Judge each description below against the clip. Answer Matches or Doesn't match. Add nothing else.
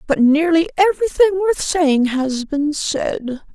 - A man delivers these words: Doesn't match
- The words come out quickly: Doesn't match